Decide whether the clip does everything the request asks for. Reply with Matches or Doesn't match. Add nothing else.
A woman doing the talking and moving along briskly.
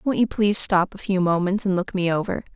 Matches